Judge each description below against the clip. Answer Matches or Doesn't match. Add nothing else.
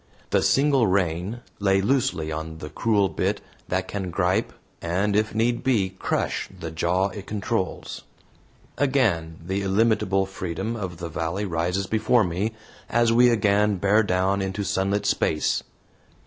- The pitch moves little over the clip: Doesn't match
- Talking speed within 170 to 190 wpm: Doesn't match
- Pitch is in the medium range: Doesn't match